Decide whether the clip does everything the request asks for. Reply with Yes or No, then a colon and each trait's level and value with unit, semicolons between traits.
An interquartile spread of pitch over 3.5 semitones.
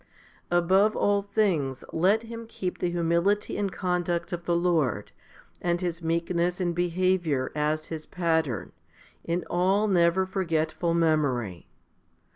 No: narrow, 2.4 semitones